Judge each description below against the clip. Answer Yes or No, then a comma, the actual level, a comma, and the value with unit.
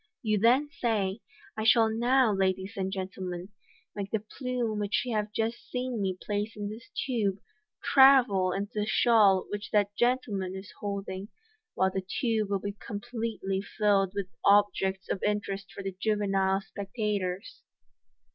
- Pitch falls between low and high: No, high, 205 Hz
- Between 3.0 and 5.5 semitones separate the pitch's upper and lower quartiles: No, narrow, 2.5 semitones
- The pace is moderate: Yes, average, 155 wpm